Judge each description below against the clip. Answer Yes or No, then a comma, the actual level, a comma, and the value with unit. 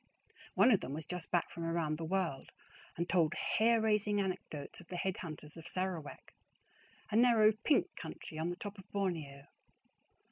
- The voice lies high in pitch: No, medium, 180 Hz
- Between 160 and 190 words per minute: Yes, average, 175 wpm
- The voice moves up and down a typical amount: Yes, average, 4.2 semitones